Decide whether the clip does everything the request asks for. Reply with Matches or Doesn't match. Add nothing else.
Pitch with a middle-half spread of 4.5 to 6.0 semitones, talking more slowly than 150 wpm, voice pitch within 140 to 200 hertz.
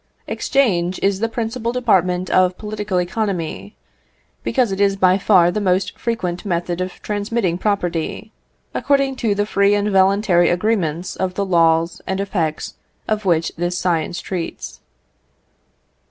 Doesn't match